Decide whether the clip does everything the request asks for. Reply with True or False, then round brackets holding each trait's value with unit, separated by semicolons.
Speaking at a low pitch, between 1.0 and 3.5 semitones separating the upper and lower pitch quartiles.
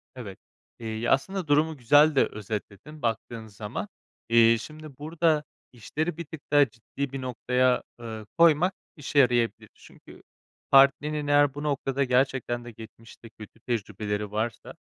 False (130 Hz; 4.6 semitones)